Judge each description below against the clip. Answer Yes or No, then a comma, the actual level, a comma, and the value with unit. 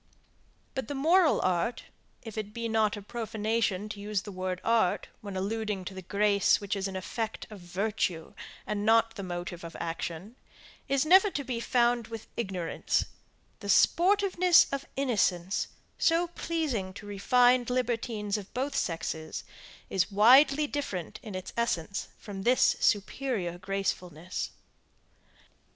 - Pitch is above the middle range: Yes, high, 210 Hz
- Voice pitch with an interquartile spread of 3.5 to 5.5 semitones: Yes, average, 4.7 semitones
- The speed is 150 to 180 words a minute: No, average, 140 wpm